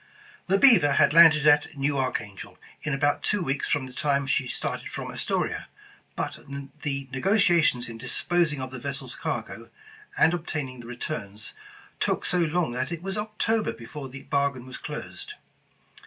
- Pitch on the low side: No, medium, 145 Hz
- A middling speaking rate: Yes, average, 160 wpm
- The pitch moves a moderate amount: Yes, average, 4.6 semitones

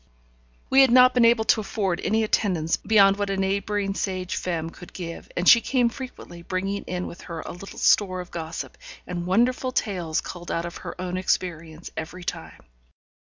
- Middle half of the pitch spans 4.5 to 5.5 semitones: No, average, 3.5 semitones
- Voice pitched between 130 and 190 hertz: Yes, medium, 185 Hz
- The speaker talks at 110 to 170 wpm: No, average, 185 wpm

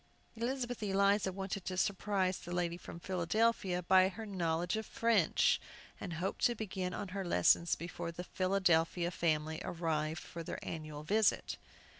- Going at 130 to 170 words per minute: Yes, average, 150 wpm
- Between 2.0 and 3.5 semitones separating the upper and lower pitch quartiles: Yes, average, 2.9 semitones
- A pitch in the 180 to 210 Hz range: Yes, medium, 185 Hz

